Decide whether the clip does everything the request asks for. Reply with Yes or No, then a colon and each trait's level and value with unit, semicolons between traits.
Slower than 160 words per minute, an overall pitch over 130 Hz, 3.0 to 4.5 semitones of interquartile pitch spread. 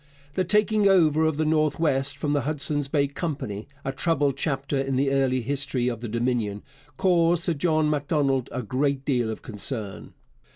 No: average, 175 wpm; medium, 140 Hz; average, 3.3 semitones